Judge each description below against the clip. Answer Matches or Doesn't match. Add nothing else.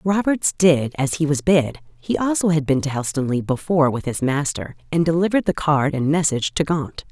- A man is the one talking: Doesn't match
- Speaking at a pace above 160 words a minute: Matches